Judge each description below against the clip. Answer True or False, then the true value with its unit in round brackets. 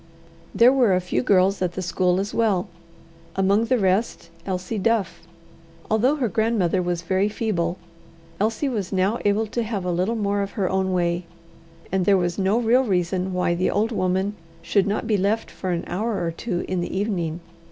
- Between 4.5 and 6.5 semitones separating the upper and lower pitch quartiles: False (3.3 semitones)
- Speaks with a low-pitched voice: False (195 Hz)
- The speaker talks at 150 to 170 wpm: False (190 wpm)